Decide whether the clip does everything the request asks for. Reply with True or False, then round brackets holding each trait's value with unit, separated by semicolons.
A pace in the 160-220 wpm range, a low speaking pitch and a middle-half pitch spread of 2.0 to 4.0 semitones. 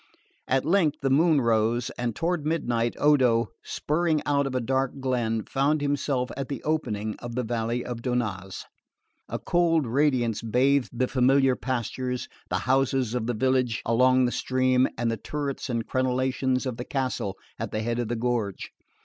True (170 wpm; 130 Hz; 2.7 semitones)